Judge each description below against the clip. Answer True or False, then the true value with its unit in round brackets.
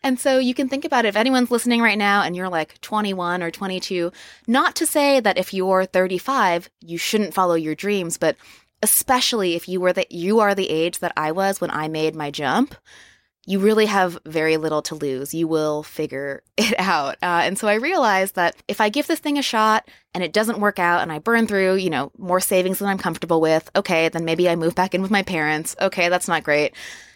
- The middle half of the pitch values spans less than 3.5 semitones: False (4.3 semitones)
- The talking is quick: True (230 wpm)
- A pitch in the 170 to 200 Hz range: True (185 Hz)